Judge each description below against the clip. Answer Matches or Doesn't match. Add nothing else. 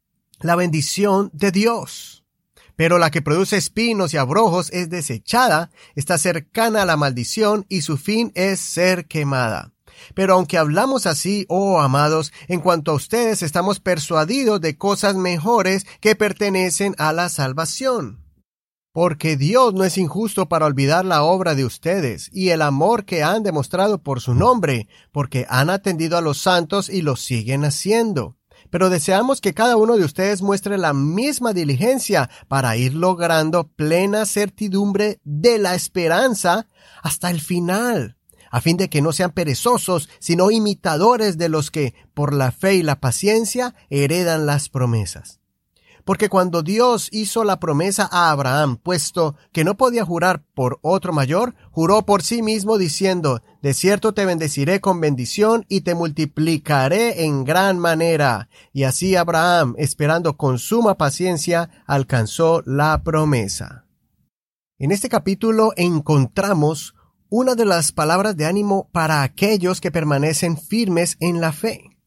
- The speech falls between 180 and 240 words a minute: Doesn't match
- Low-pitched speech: Doesn't match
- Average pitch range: Matches